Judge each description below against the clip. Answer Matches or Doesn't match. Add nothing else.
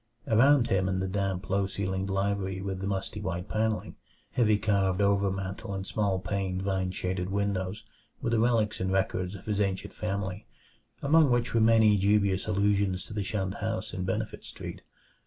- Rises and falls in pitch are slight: Matches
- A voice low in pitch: Matches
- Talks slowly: Doesn't match